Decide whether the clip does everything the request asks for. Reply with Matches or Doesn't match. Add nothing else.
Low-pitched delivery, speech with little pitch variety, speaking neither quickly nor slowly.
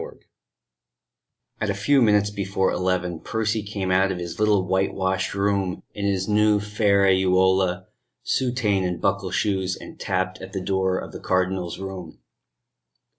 Matches